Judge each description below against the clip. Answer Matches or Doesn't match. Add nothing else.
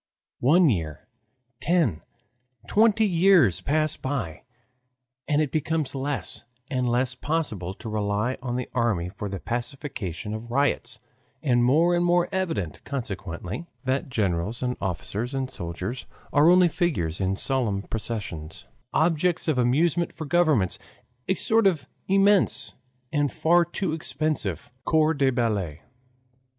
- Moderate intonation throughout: Doesn't match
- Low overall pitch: Matches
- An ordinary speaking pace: Doesn't match